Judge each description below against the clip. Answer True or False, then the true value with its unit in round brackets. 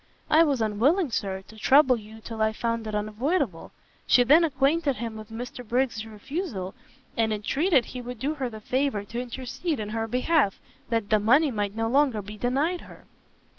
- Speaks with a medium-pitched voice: False (235 Hz)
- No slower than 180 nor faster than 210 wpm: True (185 wpm)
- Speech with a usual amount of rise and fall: True (4.3 semitones)